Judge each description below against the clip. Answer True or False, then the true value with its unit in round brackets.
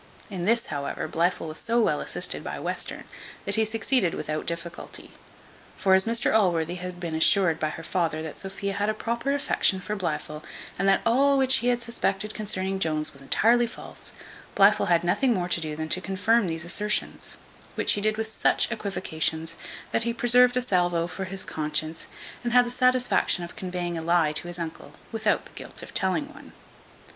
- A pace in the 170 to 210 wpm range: True (190 wpm)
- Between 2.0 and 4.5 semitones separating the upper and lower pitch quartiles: False (5.2 semitones)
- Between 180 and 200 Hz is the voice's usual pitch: True (190 Hz)